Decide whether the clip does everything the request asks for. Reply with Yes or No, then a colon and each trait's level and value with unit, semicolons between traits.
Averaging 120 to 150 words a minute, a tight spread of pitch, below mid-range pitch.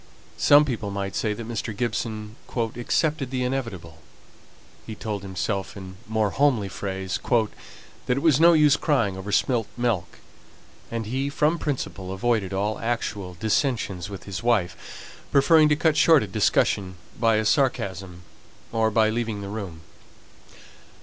No: average, 145 wpm; average, 4.4 semitones; low, 110 Hz